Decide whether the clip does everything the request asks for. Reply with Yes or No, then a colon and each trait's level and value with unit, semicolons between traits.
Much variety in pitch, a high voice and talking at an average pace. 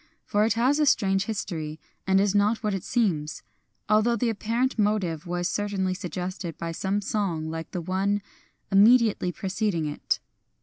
No: average, 3.4 semitones; high, 195 Hz; average, 165 wpm